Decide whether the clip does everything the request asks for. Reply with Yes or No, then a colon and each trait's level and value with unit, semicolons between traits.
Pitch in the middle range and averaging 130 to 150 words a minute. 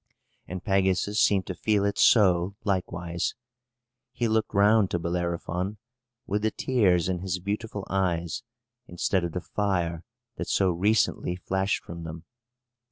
No: very low, 95 Hz; average, 140 wpm